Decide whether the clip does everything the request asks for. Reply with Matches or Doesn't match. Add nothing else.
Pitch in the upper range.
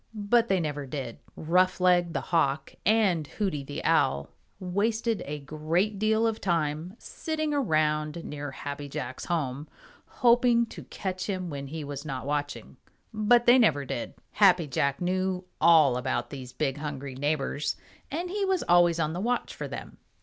Doesn't match